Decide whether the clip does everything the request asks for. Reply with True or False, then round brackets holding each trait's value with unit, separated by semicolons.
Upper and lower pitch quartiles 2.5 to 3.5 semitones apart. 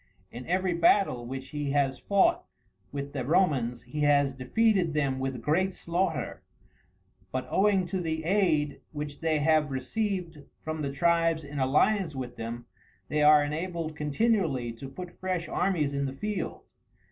False (4.5 semitones)